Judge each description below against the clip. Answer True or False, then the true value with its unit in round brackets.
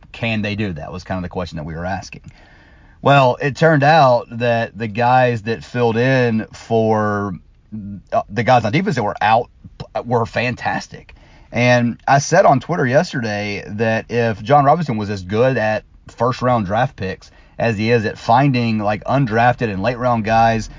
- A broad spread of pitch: False (3.3 semitones)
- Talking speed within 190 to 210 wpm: False (180 wpm)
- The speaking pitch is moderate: False (115 Hz)